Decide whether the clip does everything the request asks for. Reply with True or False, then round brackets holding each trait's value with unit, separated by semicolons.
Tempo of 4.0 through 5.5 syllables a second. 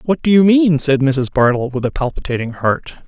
True (5.1 syllables/s)